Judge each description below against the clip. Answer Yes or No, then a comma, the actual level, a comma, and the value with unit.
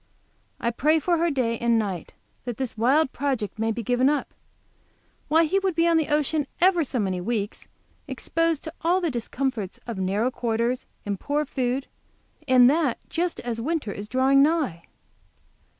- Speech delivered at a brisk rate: No, average, 170 wpm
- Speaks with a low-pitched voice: No, very high, 260 Hz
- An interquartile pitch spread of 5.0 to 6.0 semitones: Yes, wide, 5.4 semitones